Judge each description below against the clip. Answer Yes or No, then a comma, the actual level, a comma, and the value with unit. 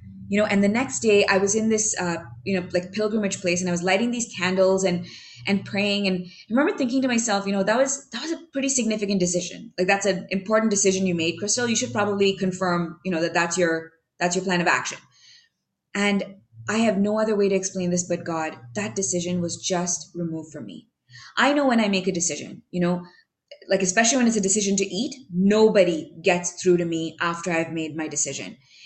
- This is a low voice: No, high, 190 Hz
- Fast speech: Yes, fast, 225 wpm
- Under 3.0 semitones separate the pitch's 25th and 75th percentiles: No, average, 3.3 semitones